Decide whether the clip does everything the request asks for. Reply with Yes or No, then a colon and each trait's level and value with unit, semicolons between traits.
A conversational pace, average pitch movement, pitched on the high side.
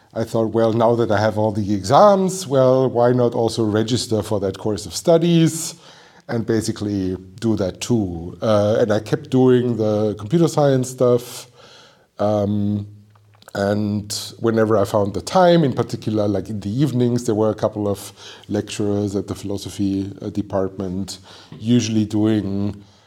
No: average, 155 wpm; average, 3.1 semitones; low, 110 Hz